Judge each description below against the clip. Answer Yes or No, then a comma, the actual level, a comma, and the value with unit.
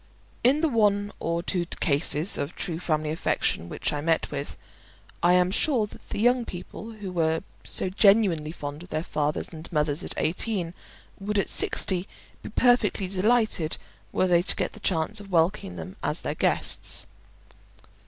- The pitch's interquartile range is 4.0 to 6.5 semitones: Yes, average, 4.6 semitones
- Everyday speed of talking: Yes, average, 170 wpm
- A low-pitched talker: No, medium, 180 Hz